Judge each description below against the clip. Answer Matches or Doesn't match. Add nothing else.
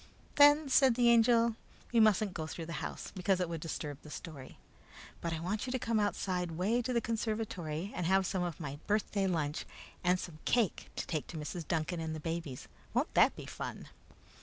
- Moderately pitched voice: Matches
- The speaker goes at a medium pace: Doesn't match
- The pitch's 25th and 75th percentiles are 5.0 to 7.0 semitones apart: Matches